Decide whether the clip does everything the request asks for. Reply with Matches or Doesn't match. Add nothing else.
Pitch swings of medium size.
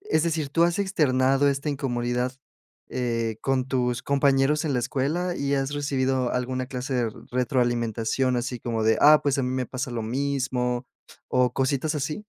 Doesn't match